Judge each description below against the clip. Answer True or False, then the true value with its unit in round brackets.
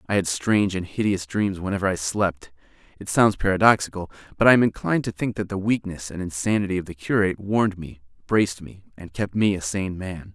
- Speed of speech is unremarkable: False (210 wpm)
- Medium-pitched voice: False (95 Hz)